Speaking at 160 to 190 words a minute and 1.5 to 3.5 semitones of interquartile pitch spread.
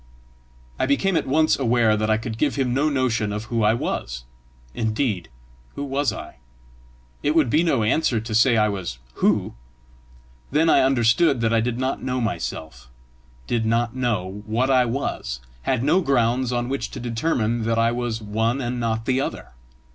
Yes: average, 180 wpm; average, 3.2 semitones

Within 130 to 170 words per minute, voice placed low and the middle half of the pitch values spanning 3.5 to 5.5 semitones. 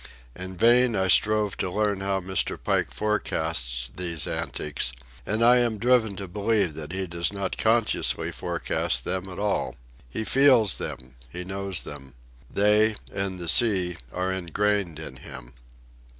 Yes: average, 150 wpm; very low, 95 Hz; average, 3.9 semitones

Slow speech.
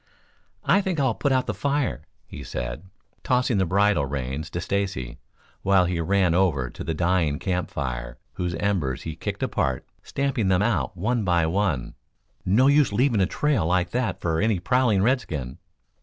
No: average, 170 wpm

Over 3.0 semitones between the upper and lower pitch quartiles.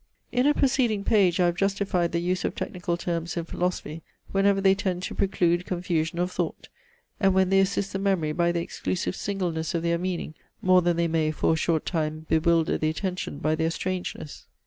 No: narrow, 2.5 semitones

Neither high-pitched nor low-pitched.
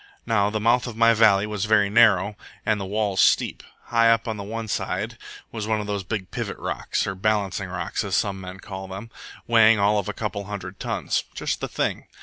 No: low, 105 Hz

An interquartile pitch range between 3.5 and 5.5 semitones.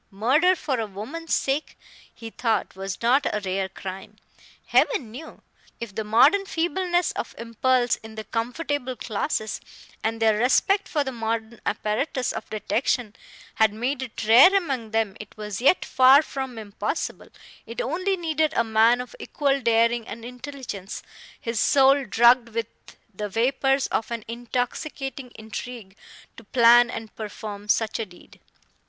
Yes: average, 3.8 semitones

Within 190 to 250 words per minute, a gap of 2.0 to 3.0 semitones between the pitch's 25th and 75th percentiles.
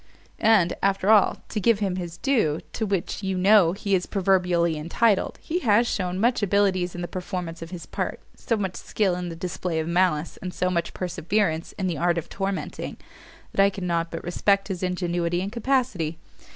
Yes: average, 195 wpm; average, 2.7 semitones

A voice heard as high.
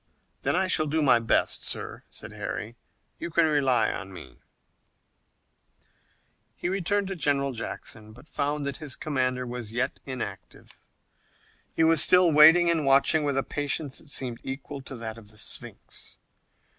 No: medium, 140 Hz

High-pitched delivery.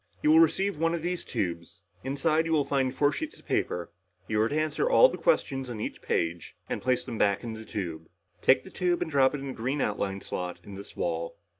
No: low, 130 Hz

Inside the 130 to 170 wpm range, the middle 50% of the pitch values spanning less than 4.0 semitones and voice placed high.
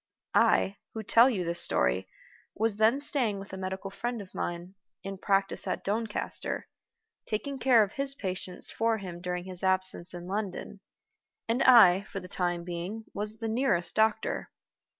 Yes: average, 165 wpm; average, 3.5 semitones; high, 195 Hz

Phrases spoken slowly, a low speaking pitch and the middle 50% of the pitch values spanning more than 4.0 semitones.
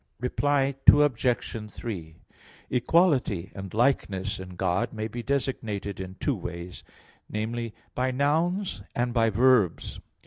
Yes: slow, 115 wpm; low, 115 Hz; average, 5.2 semitones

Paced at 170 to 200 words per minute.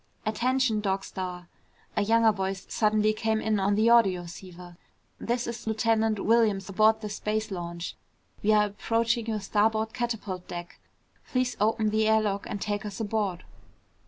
No: average, 155 wpm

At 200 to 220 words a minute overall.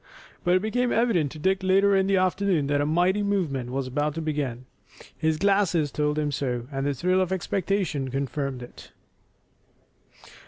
No: average, 170 wpm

